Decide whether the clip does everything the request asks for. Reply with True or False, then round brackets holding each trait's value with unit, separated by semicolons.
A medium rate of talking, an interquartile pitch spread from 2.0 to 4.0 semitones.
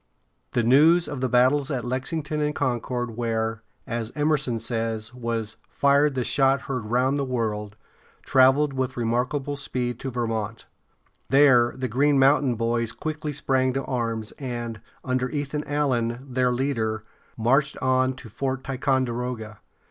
True (150 wpm; 2.8 semitones)